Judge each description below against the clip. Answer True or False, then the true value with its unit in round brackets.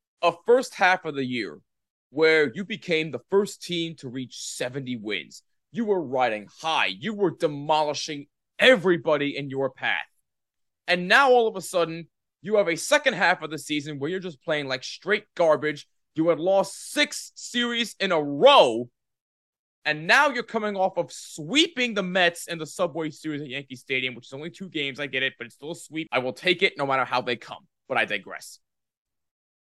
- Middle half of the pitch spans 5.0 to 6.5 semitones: True (5.5 semitones)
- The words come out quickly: False (195 wpm)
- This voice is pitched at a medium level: True (160 Hz)